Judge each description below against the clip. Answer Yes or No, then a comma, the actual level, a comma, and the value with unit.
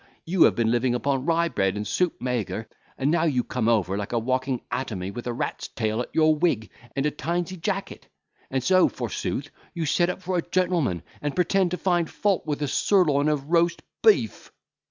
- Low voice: No, medium, 145 Hz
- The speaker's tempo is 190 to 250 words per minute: Yes, average, 200 wpm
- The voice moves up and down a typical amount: No, wide, 6.1 semitones